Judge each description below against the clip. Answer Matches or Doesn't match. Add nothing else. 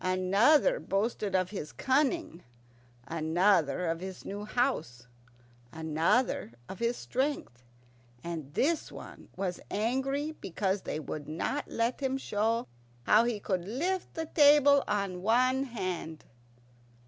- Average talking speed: Doesn't match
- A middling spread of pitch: Doesn't match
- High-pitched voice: Matches